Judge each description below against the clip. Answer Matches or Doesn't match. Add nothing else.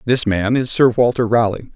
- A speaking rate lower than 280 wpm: Matches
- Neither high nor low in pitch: Doesn't match